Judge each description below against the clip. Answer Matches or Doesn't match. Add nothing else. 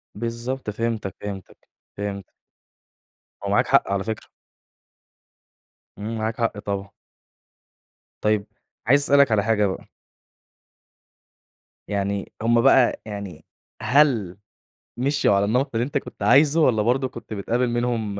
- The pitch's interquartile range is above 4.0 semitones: Doesn't match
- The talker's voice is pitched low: Matches